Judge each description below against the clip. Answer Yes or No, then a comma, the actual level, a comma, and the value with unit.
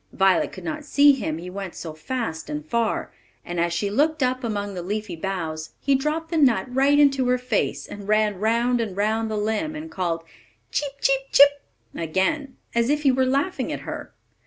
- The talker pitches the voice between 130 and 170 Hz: No, high, 230 Hz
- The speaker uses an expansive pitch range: Yes, wide, 6.4 semitones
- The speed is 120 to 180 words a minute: No, average, 200 wpm